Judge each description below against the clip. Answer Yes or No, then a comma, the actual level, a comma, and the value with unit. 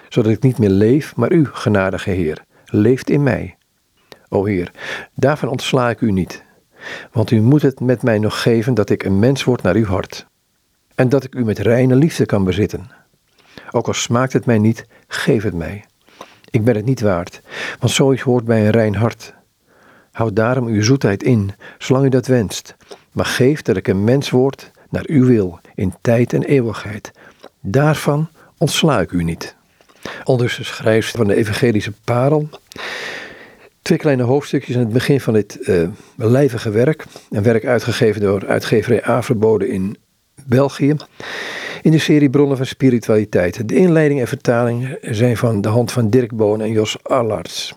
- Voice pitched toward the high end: No, low, 120 Hz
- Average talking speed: Yes, average, 175 wpm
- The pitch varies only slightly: No, average, 4.3 semitones